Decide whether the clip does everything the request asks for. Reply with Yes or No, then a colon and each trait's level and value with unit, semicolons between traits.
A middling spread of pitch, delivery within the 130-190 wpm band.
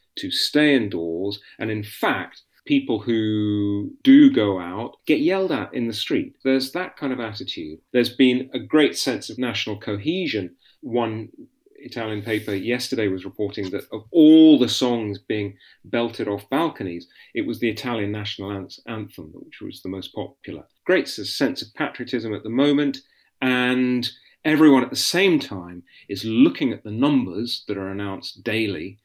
Yes: average, 4.9 semitones; average, 160 wpm